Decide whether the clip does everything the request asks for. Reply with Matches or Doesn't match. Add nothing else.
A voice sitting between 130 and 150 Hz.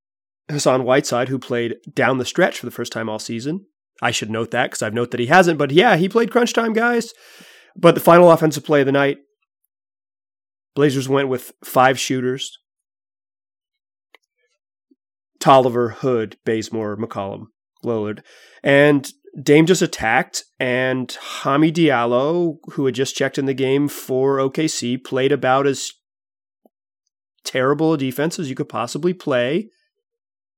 Matches